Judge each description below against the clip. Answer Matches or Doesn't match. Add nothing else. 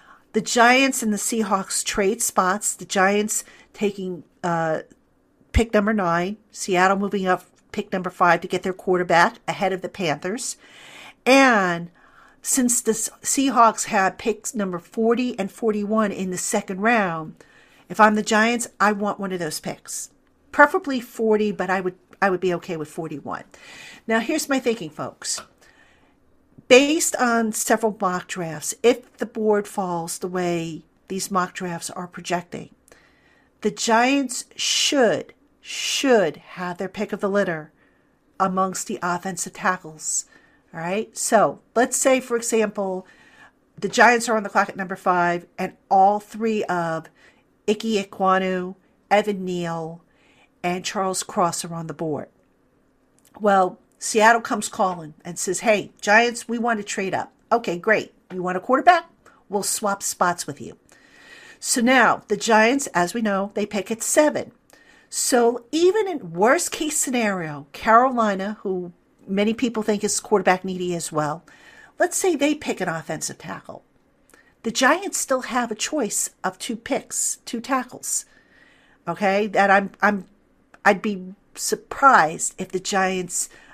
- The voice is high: Matches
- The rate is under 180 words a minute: Matches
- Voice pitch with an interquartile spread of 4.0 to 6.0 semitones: Matches